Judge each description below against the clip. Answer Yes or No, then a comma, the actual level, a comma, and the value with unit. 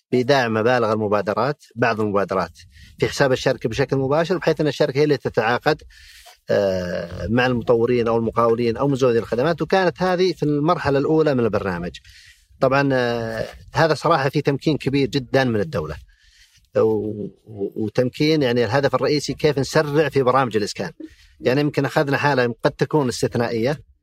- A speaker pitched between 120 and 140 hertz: Yes, low, 135 Hz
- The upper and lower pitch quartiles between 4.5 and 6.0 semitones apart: Yes, average, 5.0 semitones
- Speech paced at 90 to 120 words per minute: No, fast, 135 wpm